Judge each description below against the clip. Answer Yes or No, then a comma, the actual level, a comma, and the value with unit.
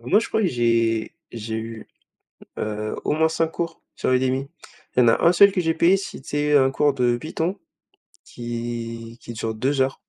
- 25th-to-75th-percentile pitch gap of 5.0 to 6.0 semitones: Yes, wide, 5.6 semitones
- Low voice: Yes, low, 130 Hz